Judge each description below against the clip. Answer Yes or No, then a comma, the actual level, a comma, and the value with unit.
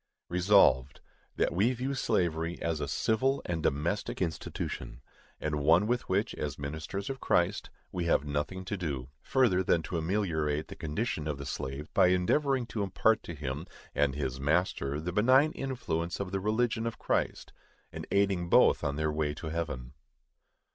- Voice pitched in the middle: No, very low, 85 Hz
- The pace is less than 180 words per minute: Yes, average, 170 wpm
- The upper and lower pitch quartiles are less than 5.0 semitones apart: No, wide, 5.5 semitones